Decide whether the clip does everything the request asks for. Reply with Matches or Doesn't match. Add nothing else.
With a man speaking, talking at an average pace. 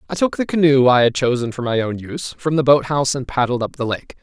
Doesn't match